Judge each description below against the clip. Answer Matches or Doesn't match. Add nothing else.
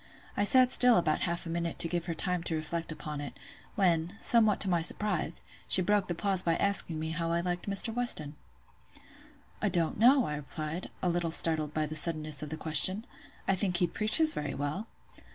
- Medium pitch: Matches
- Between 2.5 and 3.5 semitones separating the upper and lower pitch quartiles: Doesn't match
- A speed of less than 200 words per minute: Doesn't match